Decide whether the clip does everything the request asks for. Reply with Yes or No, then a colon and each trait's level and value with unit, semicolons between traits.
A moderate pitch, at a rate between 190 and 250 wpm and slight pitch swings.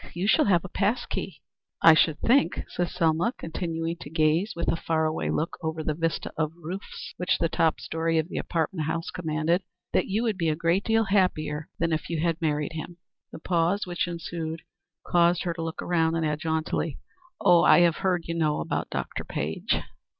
Yes: medium, 165 Hz; average, 200 wpm; narrow, 1.9 semitones